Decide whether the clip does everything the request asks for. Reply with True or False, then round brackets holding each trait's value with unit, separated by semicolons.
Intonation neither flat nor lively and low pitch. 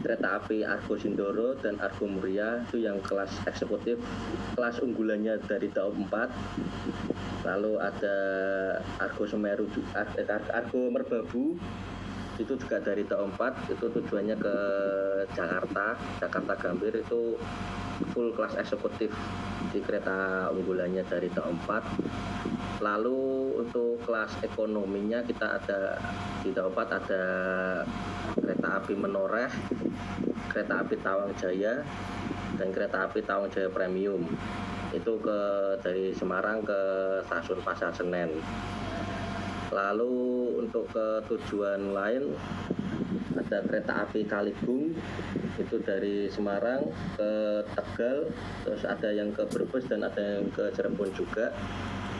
False (1.9 semitones; 100 Hz)